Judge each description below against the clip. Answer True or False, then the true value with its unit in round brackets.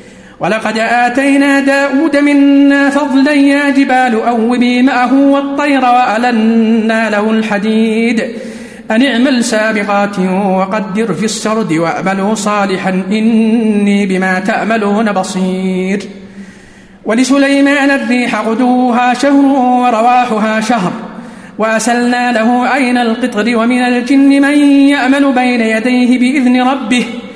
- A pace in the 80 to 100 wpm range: True (95 wpm)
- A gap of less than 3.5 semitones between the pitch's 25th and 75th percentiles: True (2.9 semitones)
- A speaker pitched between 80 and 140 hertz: False (235 Hz)